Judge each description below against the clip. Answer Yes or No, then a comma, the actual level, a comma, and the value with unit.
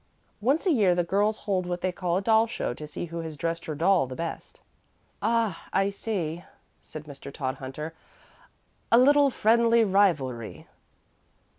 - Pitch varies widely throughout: Yes, wide, 6.0 semitones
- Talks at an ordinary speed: Yes, average, 160 wpm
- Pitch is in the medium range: Yes, medium, 180 Hz